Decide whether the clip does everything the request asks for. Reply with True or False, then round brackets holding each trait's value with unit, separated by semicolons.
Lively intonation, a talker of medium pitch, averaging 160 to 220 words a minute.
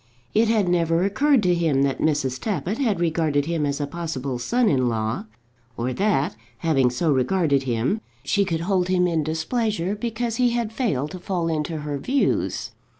True (6.4 semitones; 165 Hz; 180 wpm)